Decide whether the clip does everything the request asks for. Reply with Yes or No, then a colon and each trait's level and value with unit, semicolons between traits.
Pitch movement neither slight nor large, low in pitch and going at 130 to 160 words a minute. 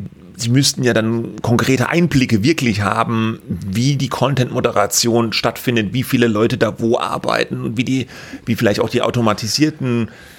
No: narrow, 2.2 semitones; low, 120 Hz; average, 155 wpm